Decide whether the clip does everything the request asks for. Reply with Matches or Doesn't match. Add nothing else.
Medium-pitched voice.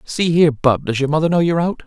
Matches